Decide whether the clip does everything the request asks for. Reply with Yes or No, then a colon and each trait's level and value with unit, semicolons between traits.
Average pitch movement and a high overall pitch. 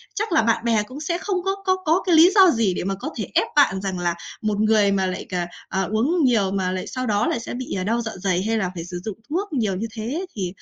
No: wide, 7.4 semitones; high, 220 Hz